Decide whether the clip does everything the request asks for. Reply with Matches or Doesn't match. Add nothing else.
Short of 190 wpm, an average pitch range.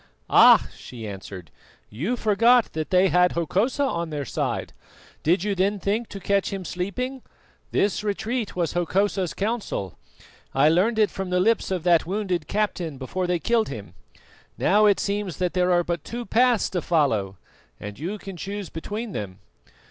Matches